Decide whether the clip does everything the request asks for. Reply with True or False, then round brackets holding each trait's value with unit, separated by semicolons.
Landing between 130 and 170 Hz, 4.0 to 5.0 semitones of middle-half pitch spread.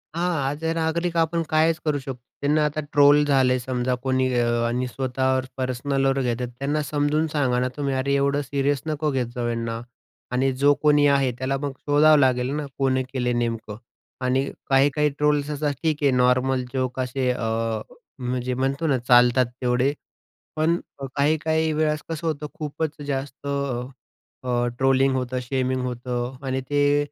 False (135 Hz; 2.6 semitones)